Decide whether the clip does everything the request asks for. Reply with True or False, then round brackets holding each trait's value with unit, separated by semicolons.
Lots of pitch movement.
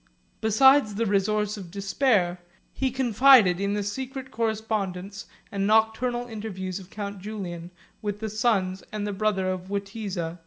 False (2.4 semitones)